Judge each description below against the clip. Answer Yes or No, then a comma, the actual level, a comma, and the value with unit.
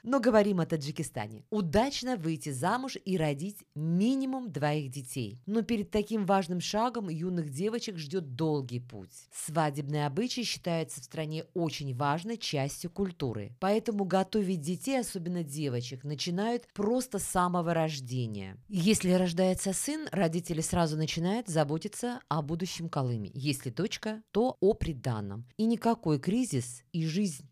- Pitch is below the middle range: No, medium, 175 Hz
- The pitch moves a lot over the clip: Yes, wide, 6.1 semitones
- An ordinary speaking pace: Yes, average, 135 wpm